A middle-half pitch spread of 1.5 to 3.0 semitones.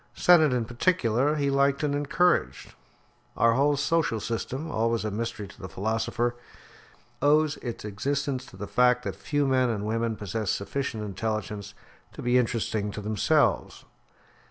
No: average, 4.5 semitones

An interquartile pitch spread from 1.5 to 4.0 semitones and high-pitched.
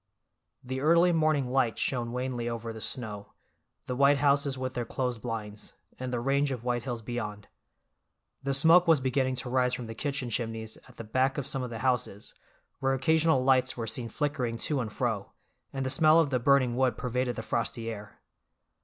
No: average, 2.9 semitones; low, 125 Hz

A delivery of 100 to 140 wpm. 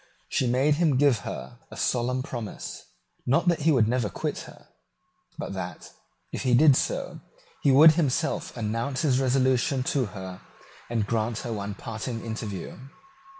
No: average, 155 wpm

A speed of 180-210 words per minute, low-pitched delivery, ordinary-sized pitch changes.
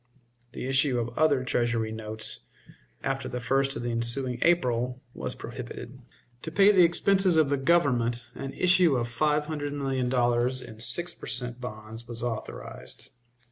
No: average, 160 wpm; low, 125 Hz; average, 3.8 semitones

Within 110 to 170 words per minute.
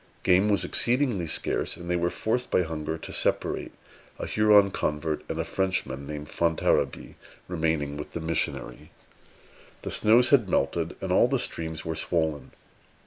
Yes: average, 155 wpm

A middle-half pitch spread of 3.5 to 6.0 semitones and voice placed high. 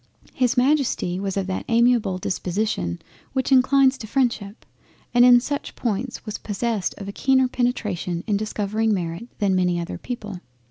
Yes: average, 4.4 semitones; high, 220 Hz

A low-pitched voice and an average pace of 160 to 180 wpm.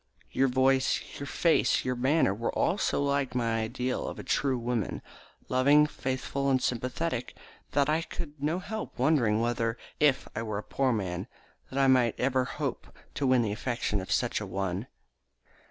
Yes: low, 130 Hz; average, 170 wpm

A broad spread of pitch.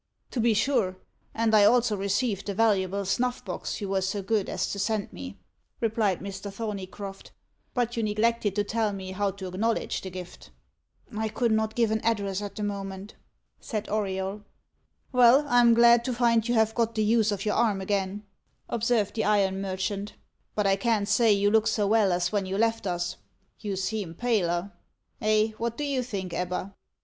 No: average, 2.7 semitones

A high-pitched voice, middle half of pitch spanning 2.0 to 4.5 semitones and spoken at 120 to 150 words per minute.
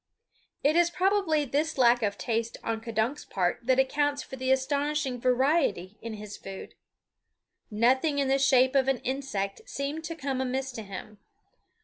No: very high, 265 Hz; average, 4.0 semitones; average, 160 wpm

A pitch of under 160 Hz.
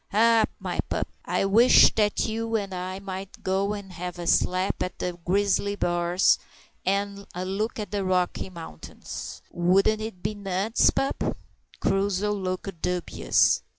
No: high, 195 Hz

